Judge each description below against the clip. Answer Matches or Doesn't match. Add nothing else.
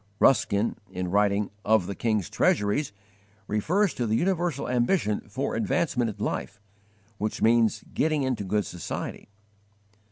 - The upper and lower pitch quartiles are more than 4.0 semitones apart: Matches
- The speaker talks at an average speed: Doesn't match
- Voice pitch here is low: Matches